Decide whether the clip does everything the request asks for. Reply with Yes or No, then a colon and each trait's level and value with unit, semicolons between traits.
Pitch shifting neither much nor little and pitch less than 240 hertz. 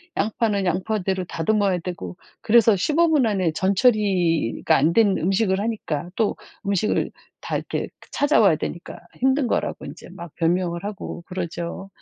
Yes: average, 4.0 semitones; high, 190 Hz